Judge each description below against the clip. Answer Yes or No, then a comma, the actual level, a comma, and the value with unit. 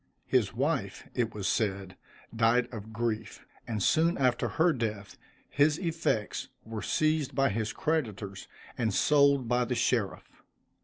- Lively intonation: No, average, 4.8 semitones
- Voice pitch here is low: Yes, low, 120 Hz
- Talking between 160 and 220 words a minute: No, average, 140 wpm